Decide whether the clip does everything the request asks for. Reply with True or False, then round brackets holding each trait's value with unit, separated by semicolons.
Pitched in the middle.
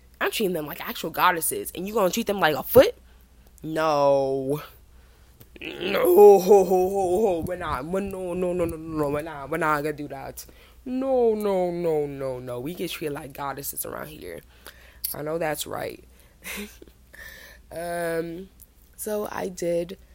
True (170 Hz)